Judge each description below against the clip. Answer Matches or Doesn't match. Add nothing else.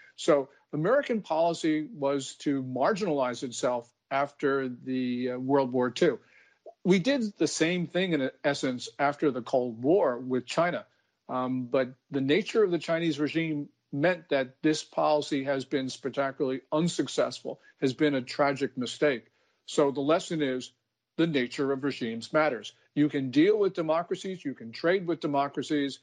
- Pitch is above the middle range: Doesn't match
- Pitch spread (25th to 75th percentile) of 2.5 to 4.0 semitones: Matches